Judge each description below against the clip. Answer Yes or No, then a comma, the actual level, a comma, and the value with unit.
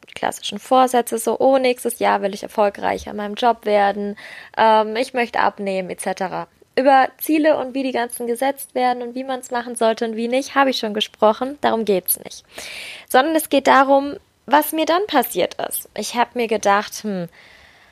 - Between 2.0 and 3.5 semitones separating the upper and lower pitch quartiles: No, average, 3.9 semitones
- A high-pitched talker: Yes, high, 240 Hz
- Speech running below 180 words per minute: No, fast, 190 wpm